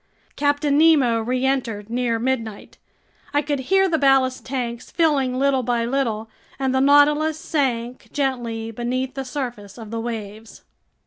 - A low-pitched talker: No, very high, 255 Hz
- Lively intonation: No, average, 3.4 semitones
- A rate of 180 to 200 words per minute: No, average, 140 wpm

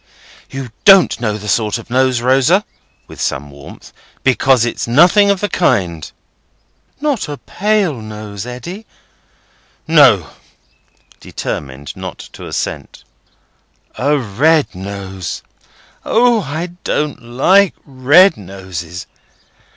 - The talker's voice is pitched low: Yes, low, 130 Hz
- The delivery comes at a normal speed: No, slow, 110 wpm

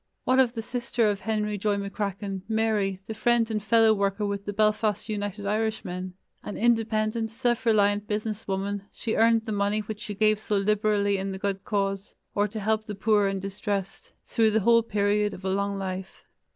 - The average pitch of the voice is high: Yes, high, 210 Hz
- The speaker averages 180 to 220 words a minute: Yes, average, 190 wpm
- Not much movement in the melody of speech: Yes, narrow, 1.7 semitones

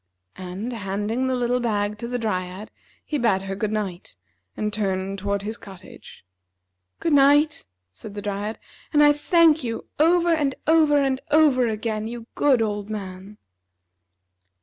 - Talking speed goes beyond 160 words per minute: No, average, 150 wpm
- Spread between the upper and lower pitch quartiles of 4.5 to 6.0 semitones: Yes, wide, 5.5 semitones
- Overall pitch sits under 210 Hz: No, high, 225 Hz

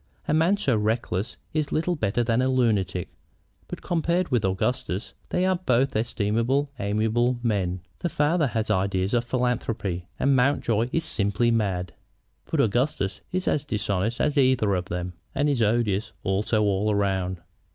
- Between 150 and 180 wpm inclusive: Yes, average, 155 wpm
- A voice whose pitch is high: No, low, 115 Hz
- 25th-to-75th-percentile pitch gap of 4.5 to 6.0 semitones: Yes, average, 5.2 semitones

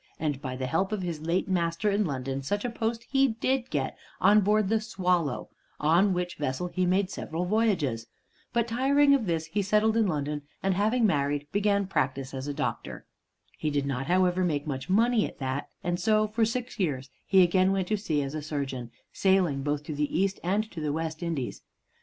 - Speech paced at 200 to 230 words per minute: Yes, fast, 205 wpm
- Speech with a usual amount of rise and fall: No, wide, 6.2 semitones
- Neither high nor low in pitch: Yes, medium, 180 Hz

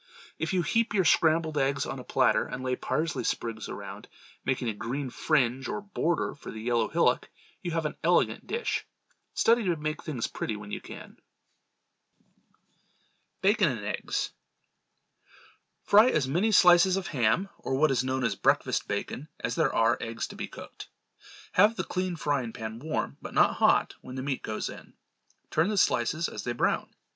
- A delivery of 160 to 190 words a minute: Yes, average, 180 wpm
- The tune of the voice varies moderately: No, wide, 6.4 semitones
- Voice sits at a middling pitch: Yes, medium, 145 Hz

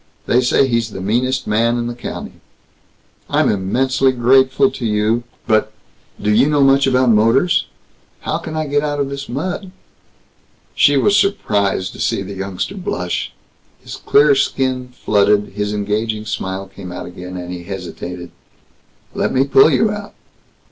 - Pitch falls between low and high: No, low, 120 Hz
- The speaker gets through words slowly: No, average, 155 wpm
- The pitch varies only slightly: No, average, 5.2 semitones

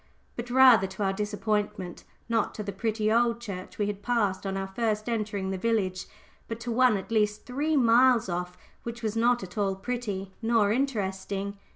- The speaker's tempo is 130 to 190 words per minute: Yes, average, 180 wpm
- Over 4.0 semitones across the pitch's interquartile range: No, average, 3.2 semitones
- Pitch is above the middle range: Yes, high, 215 Hz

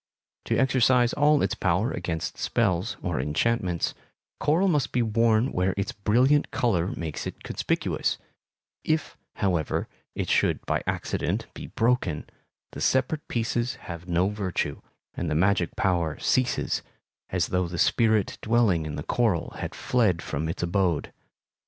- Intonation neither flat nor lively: No, wide, 5.8 semitones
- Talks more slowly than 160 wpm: Yes, average, 145 wpm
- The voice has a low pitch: Yes, low, 100 Hz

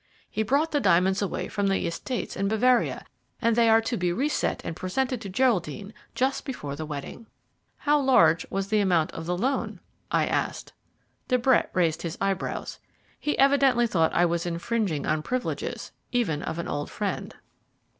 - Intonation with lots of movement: Yes, wide, 6.7 semitones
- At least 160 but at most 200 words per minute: Yes, average, 180 wpm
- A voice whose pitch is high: Yes, high, 200 Hz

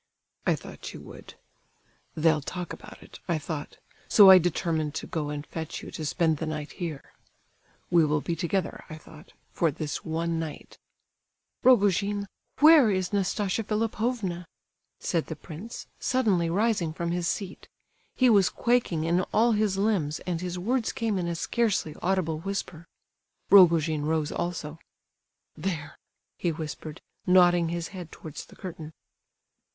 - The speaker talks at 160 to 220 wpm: No, average, 145 wpm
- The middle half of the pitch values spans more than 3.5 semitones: Yes, average, 3.9 semitones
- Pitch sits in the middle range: Yes, medium, 175 Hz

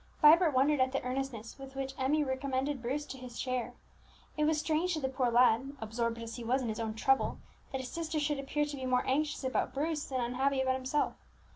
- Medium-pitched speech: No, very high, 265 Hz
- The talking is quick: Yes, fast, 225 wpm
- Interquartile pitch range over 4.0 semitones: No, average, 2.7 semitones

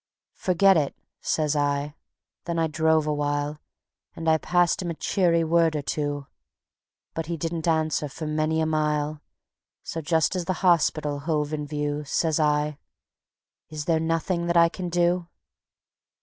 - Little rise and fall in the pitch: Yes, narrow, 2.1 semitones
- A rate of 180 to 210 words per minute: No, average, 155 wpm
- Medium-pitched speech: Yes, medium, 160 Hz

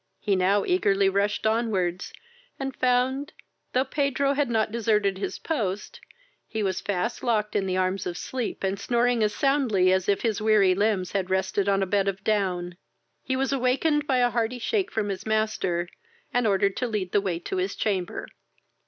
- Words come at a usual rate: Yes, average, 190 wpm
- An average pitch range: Yes, average, 4.3 semitones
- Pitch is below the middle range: No, high, 210 Hz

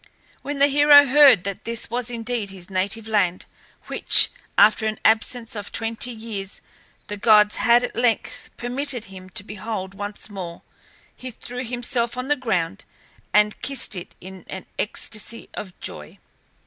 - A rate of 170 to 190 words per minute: No, average, 155 wpm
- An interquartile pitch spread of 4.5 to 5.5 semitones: No, average, 3.7 semitones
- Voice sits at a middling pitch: No, high, 220 Hz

